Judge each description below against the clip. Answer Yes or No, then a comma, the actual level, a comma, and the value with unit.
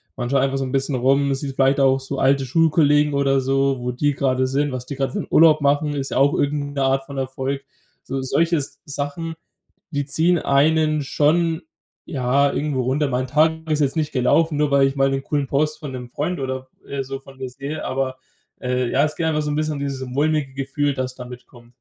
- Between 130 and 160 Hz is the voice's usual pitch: Yes, medium, 140 Hz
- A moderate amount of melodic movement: No, narrow, 1.9 semitones